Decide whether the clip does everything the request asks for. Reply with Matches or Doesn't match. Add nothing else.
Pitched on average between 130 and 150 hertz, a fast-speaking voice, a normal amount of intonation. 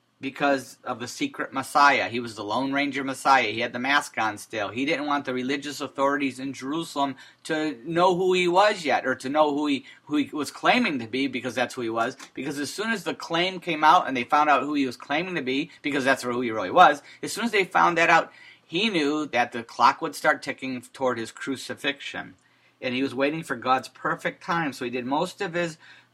Matches